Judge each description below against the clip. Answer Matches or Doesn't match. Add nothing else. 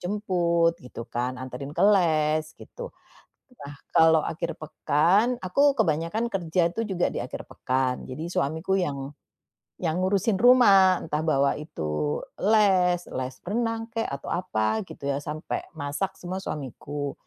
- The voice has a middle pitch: Matches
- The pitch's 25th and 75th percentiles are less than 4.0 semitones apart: Doesn't match